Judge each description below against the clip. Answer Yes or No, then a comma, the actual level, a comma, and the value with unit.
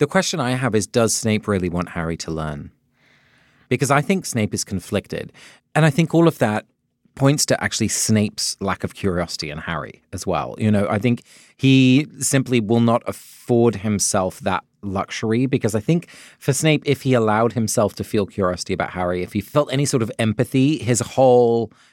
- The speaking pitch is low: Yes, low, 115 Hz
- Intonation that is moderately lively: Yes, average, 4.8 semitones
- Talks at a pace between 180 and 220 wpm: Yes, average, 190 wpm